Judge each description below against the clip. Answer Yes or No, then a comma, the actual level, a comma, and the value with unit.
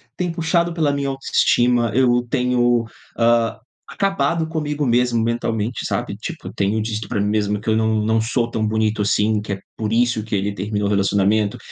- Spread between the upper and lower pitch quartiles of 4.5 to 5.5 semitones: No, average, 2.8 semitones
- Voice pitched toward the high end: No, low, 115 Hz